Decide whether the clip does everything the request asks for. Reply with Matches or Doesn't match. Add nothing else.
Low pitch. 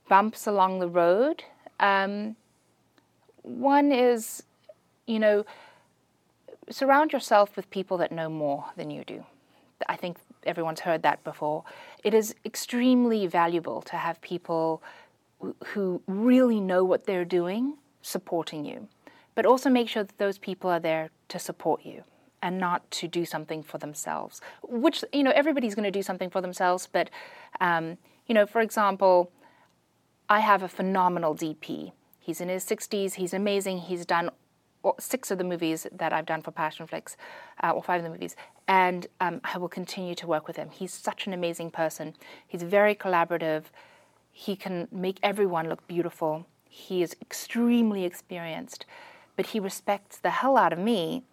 Doesn't match